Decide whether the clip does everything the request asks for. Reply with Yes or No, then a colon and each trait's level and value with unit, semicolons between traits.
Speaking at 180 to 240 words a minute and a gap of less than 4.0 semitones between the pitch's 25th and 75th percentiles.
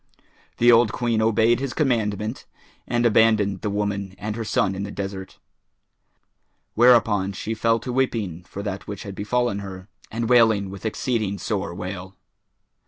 No: average, 155 wpm; average, 2.8 semitones